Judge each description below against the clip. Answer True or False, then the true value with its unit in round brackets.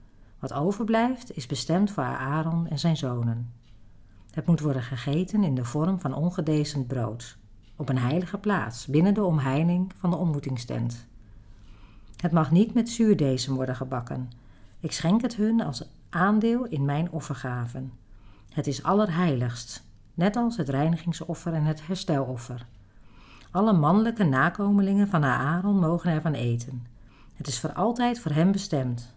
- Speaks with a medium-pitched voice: True (150 Hz)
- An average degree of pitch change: False (6.6 semitones)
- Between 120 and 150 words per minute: True (145 wpm)